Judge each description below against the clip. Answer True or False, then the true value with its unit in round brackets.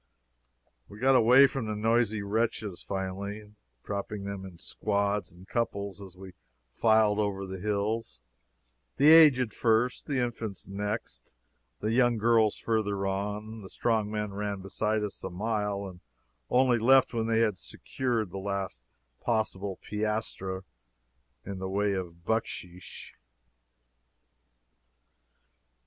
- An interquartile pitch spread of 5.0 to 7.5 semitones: False (2.5 semitones)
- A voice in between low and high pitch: False (105 Hz)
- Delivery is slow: True (130 wpm)